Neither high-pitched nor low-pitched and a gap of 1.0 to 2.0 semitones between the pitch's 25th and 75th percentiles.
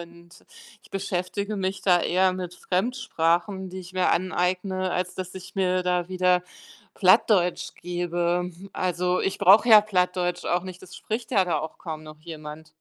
Yes: medium, 180 Hz; narrow, 1.3 semitones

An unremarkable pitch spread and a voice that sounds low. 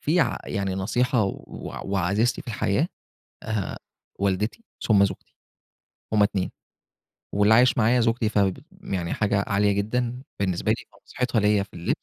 Yes: average, 3.0 semitones; low, 105 Hz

